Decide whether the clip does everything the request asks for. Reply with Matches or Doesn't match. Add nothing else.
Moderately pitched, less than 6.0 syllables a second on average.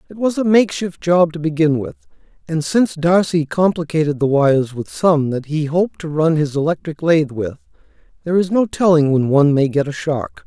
Matches